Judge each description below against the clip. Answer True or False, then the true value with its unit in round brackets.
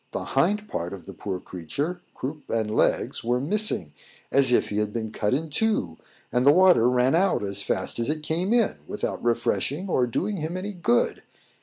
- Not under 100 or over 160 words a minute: False (185 wpm)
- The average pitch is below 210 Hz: True (135 Hz)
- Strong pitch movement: True (8.5 semitones)